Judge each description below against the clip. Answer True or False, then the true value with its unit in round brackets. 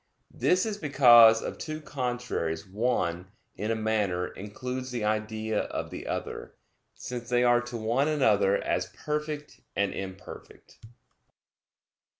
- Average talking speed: False (130 wpm)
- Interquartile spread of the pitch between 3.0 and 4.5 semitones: True (3.7 semitones)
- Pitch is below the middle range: True (120 Hz)